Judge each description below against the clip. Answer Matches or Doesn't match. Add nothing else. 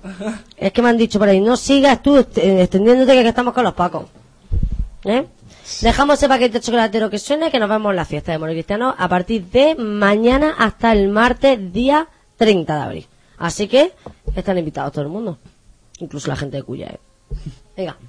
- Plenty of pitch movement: Matches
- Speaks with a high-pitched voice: Matches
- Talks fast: Matches